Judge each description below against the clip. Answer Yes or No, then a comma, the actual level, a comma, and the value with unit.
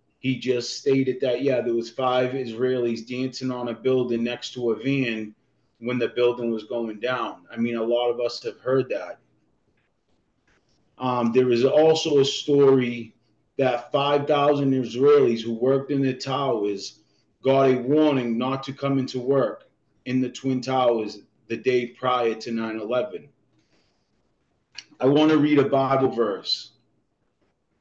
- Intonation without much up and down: Yes, narrow, 2.3 semitones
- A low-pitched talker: Yes, low, 125 Hz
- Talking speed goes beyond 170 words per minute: No, average, 150 wpm